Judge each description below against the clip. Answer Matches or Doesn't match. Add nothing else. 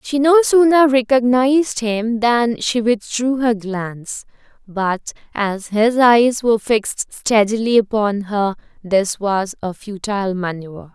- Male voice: Doesn't match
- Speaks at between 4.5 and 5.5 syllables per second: Doesn't match